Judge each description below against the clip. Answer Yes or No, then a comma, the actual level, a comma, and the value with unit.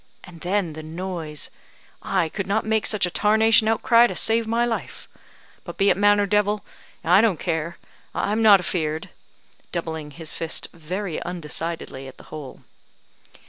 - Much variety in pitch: No, average, 4.5 semitones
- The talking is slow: No, average, 160 wpm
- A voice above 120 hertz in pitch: Yes, medium, 185 Hz